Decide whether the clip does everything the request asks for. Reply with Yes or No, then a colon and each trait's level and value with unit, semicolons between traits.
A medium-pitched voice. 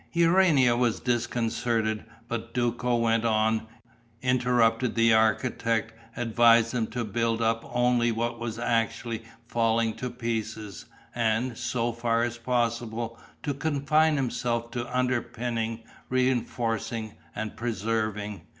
No: low, 115 Hz